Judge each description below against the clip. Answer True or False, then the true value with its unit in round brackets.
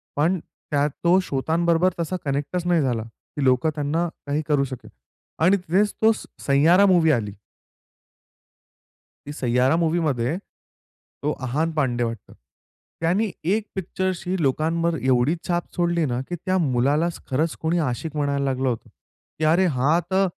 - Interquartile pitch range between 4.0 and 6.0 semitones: True (4.3 semitones)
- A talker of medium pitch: True (155 Hz)